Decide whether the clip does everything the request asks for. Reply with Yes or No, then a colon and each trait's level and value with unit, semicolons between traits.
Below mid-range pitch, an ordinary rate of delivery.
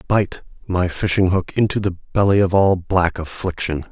Yes: very low, 95 Hz; average, 170 wpm